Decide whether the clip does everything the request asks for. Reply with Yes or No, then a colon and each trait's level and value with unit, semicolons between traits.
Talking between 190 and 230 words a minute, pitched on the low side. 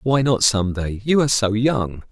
Yes: average, 200 wpm; low, 115 Hz